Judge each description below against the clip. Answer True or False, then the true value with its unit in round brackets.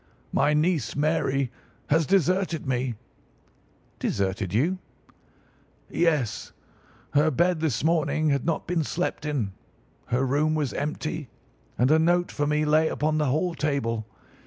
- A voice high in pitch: False (150 Hz)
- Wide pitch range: False (3.2 semitones)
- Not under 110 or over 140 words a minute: True (135 wpm)